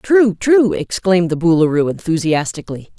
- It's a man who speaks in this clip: No, female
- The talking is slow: Yes, slow, 100 wpm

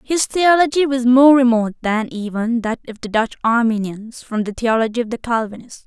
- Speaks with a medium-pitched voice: No, high, 235 Hz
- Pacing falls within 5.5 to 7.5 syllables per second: No, 5.2 syllables/s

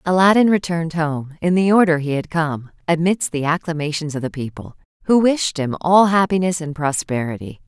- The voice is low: No, medium, 165 Hz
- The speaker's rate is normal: Yes, average, 170 wpm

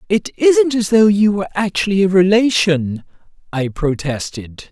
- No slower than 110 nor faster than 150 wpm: Yes, average, 140 wpm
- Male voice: Yes, male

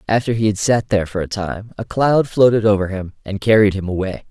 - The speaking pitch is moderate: No, low, 105 Hz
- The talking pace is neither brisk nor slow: No, fast, 235 wpm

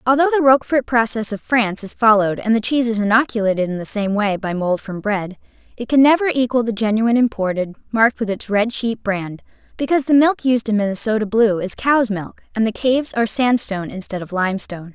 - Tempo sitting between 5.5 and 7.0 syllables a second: Yes, 6.1 syllables/s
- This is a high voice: Yes, high, 225 Hz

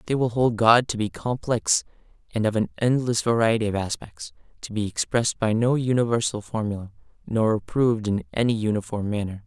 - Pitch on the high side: No, low, 115 Hz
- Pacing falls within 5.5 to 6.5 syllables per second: Yes, 5.6 syllables/s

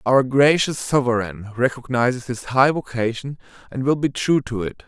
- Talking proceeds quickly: No, average, 160 wpm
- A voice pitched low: Yes, low, 125 Hz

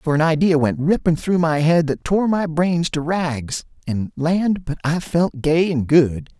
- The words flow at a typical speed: Yes, average, 195 wpm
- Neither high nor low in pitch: Yes, medium, 160 Hz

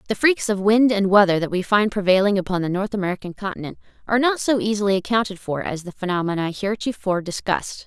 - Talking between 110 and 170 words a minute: No, average, 200 wpm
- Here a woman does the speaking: Yes, female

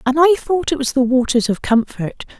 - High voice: Yes, very high, 270 Hz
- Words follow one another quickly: Yes, fast, 225 wpm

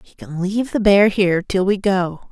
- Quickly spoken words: Yes, fast, 235 wpm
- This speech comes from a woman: Yes, female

